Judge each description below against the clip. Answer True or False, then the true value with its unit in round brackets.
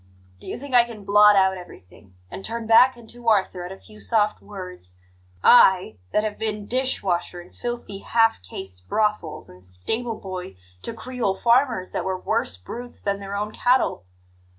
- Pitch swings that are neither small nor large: True (4.2 semitones)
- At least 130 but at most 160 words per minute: False (175 wpm)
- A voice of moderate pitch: False (205 Hz)